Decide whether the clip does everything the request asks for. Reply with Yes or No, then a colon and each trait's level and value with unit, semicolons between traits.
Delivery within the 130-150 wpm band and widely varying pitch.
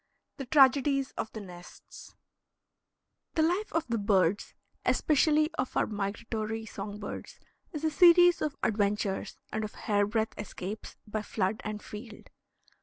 Yes: average, 140 wpm; wide, 5.7 semitones